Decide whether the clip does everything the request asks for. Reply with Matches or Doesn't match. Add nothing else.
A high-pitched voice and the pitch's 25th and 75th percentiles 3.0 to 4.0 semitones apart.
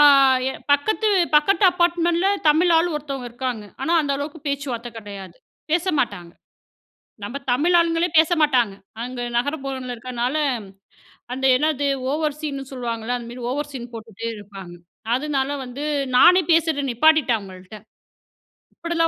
Doesn't match